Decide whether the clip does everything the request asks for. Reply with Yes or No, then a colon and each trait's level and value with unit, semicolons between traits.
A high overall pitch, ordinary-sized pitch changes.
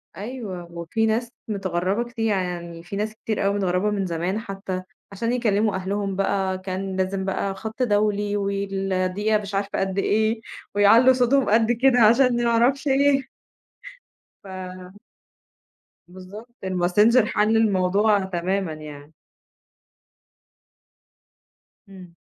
Yes: high, 200 Hz; average, 3.0 semitones